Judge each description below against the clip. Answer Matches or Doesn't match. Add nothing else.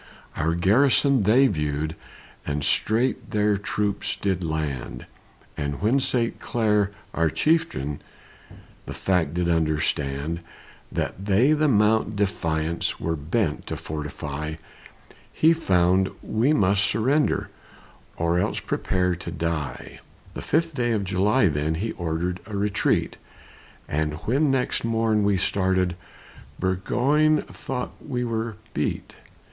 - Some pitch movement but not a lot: Doesn't match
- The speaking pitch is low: Matches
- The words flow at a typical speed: Doesn't match